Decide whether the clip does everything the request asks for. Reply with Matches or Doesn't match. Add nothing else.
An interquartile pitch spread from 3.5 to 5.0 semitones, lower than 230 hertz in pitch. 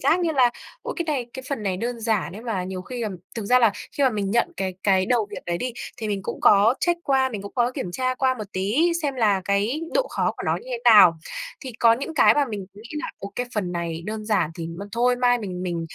Matches